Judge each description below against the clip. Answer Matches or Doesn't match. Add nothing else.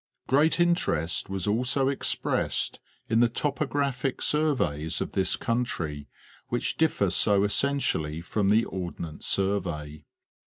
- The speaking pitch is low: Matches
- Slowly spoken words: Matches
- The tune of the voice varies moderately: Doesn't match